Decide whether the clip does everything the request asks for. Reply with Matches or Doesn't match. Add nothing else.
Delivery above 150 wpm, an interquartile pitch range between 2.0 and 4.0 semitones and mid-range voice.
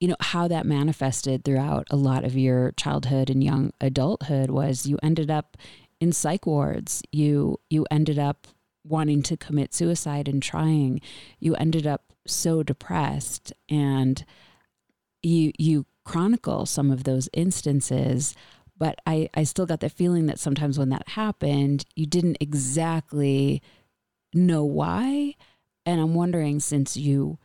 Doesn't match